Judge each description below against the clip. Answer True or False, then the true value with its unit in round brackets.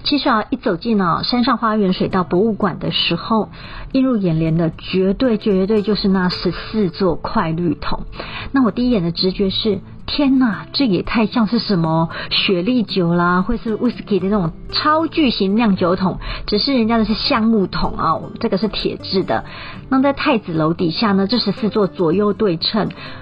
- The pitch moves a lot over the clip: False (4.4 semitones)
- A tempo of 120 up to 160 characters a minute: False (285 characters per minute)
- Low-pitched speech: False (205 Hz)